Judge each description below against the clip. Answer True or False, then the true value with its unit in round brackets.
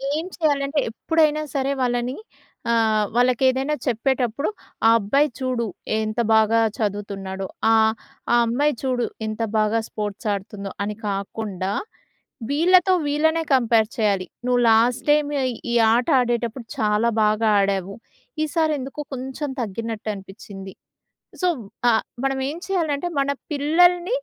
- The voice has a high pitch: True (240 Hz)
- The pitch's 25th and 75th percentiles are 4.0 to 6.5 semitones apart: True (5.1 semitones)